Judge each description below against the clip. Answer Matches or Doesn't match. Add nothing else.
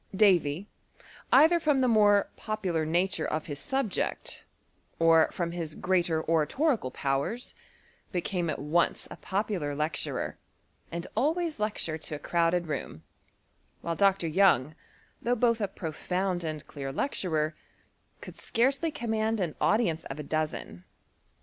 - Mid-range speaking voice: Matches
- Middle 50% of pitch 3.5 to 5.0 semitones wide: Doesn't match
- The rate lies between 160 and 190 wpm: Doesn't match